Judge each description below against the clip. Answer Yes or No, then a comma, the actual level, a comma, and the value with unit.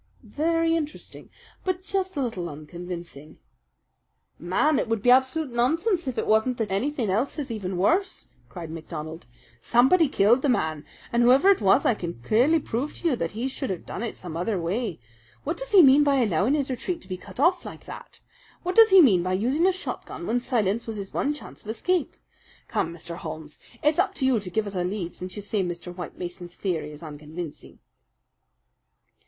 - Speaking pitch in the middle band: No, high, 225 Hz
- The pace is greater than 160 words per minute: Yes, average, 200 wpm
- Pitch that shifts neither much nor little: No, wide, 8.5 semitones